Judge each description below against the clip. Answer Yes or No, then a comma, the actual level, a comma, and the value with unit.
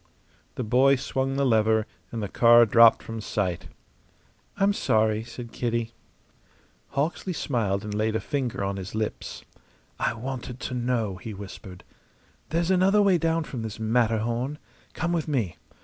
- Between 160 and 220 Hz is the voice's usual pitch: No, low, 115 Hz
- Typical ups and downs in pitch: Yes, average, 3.9 semitones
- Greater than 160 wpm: No, average, 150 wpm